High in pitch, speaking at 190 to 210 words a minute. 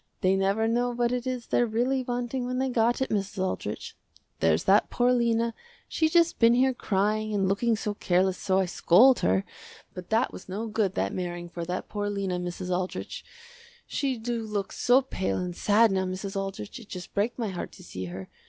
Yes: high, 210 Hz; fast, 205 wpm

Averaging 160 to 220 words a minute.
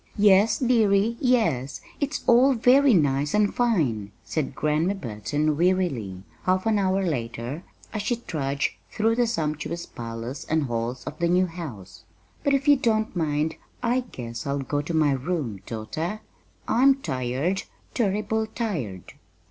No: average, 145 wpm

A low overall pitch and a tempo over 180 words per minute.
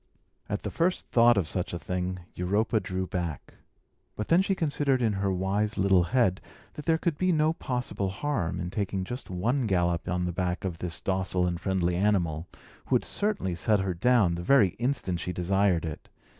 Yes: very low, 95 Hz; average, 195 wpm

